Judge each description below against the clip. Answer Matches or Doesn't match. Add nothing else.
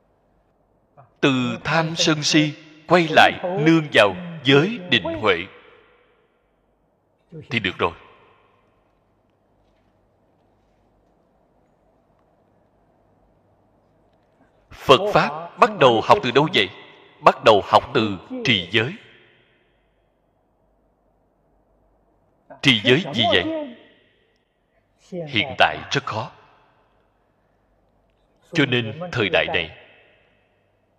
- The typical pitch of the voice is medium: Matches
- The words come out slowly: Matches